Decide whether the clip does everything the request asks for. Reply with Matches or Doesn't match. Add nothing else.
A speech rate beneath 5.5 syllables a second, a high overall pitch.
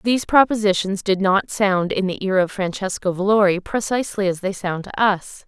Matches